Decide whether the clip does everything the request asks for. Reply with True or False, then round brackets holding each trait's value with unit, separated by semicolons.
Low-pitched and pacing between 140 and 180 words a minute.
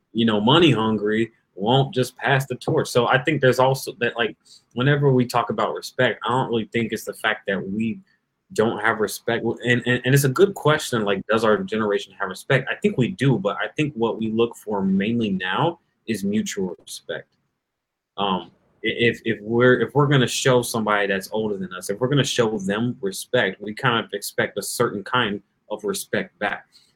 False (120 Hz; 205 wpm)